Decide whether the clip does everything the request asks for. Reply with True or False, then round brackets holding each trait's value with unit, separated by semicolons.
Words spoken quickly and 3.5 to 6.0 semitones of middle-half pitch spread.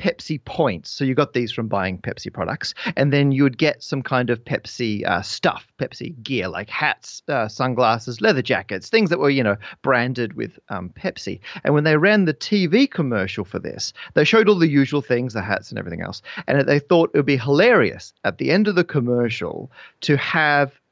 True (210 wpm; 4.1 semitones)